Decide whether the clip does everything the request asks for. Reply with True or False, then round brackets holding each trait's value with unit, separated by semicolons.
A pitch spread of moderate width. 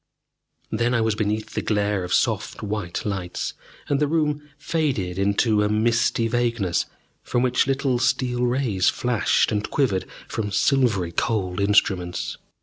True (3.8 semitones)